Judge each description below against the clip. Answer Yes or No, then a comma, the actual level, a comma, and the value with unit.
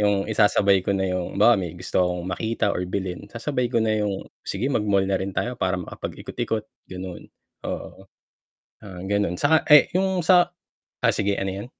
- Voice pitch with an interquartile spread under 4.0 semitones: Yes, average, 3.5 semitones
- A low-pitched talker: Yes, low, 100 Hz